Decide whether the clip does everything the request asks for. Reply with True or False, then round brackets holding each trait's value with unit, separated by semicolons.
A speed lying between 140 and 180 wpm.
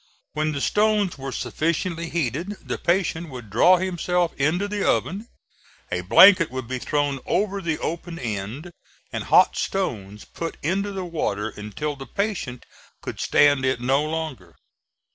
True (150 wpm)